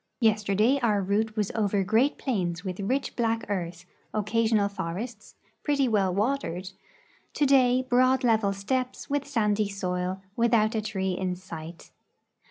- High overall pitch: Yes, high, 215 Hz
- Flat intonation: No, average, 4.3 semitones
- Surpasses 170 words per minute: No, slow, 135 wpm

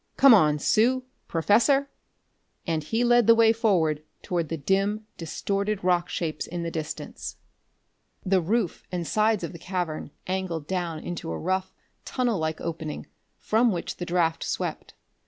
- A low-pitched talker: No, medium, 180 Hz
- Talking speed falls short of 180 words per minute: Yes, average, 155 wpm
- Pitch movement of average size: Yes, average, 4.8 semitones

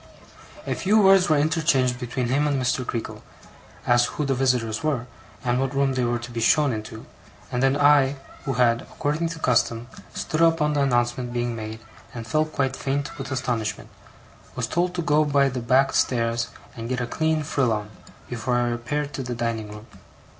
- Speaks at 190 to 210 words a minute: Yes, average, 195 wpm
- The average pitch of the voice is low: Yes, low, 130 Hz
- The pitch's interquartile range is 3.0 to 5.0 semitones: Yes, average, 3.5 semitones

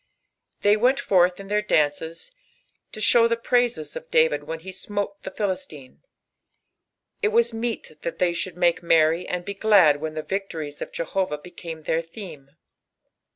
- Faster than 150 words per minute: Yes, average, 160 wpm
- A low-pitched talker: No, medium, 185 Hz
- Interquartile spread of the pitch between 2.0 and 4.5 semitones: No, average, 4.9 semitones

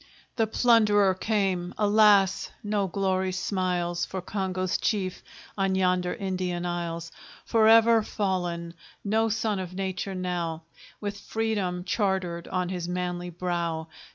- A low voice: No, medium, 185 Hz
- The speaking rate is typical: No, slow, 120 wpm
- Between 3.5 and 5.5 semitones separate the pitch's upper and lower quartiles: No, narrow, 2.5 semitones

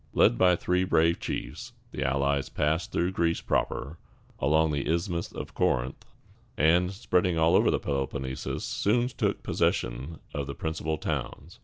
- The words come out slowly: No, average, 150 wpm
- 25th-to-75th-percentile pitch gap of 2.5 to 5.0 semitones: Yes, average, 4.1 semitones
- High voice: No, very low, 80 Hz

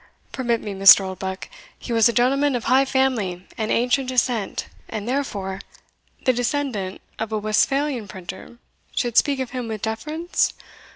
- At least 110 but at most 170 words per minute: Yes, average, 155 wpm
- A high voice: Yes, high, 235 Hz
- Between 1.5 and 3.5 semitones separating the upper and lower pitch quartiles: No, average, 4.3 semitones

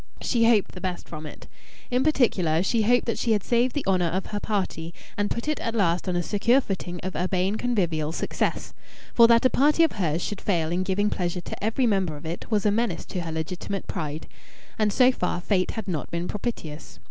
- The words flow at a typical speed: No, fast, 220 wpm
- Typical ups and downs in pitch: Yes, average, 4.9 semitones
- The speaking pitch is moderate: No, high, 195 Hz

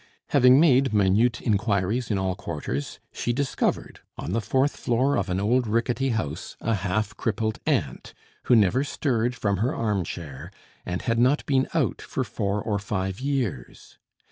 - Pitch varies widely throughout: No, average, 4.6 semitones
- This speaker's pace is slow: No, average, 165 wpm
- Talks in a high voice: No, low, 110 Hz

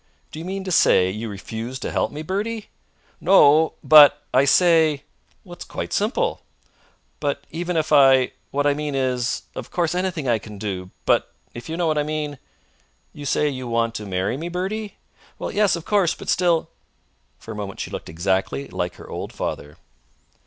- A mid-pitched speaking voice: Yes, medium, 145 Hz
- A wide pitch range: Yes, wide, 7.0 semitones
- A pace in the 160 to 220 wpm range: Yes, average, 190 wpm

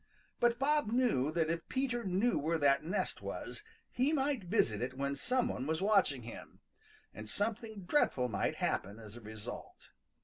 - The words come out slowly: No, average, 170 wpm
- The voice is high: No, medium, 175 Hz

